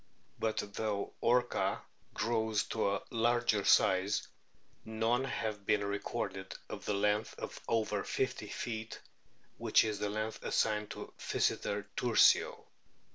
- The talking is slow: Yes, slow, 125 wpm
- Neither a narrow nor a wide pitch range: No, narrow, 1.7 semitones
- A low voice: Yes, low, 110 Hz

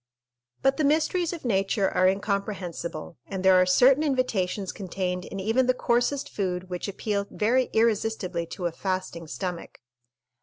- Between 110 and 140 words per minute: No, average, 150 wpm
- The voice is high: Yes, high, 195 Hz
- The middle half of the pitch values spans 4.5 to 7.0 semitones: Yes, average, 5.0 semitones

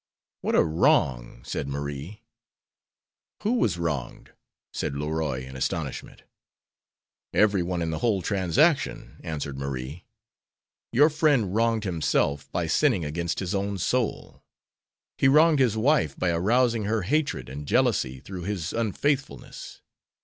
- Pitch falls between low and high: No, very low, 90 Hz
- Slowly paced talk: Yes, slow, 130 wpm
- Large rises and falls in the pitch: Yes, wide, 7.8 semitones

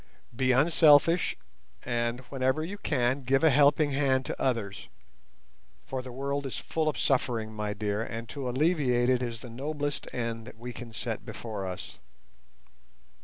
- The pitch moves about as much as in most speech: Yes, average, 3.4 semitones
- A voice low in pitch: Yes, low, 130 Hz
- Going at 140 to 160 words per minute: Yes, average, 155 wpm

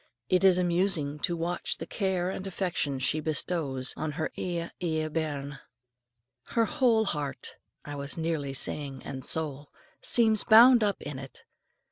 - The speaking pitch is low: No, medium, 160 Hz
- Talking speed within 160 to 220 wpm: No, average, 150 wpm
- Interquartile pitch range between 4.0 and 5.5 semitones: Yes, average, 4.7 semitones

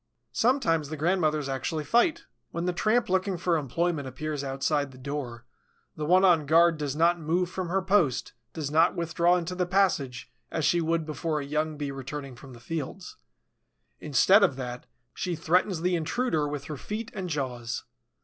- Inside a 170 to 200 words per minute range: Yes, average, 180 wpm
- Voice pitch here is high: No, medium, 160 Hz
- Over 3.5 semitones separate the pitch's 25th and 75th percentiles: Yes, average, 4.0 semitones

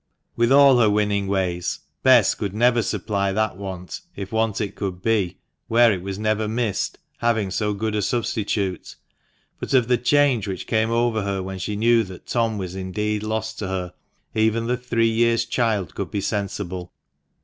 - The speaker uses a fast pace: No, average, 180 wpm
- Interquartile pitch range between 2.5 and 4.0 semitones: Yes, average, 2.9 semitones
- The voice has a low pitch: Yes, low, 105 Hz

